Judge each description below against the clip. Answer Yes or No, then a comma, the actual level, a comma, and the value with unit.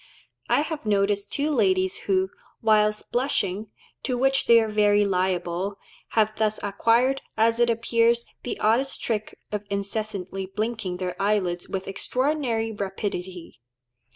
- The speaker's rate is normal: No, slow, 130 wpm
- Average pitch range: Yes, average, 3.1 semitones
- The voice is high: Yes, high, 210 Hz